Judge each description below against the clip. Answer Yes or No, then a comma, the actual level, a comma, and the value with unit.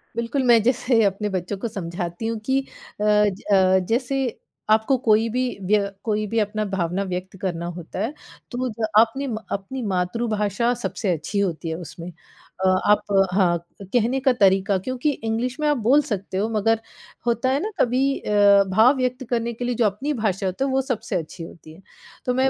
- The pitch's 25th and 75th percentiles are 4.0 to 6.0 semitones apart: Yes, average, 4.4 semitones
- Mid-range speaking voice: No, high, 215 Hz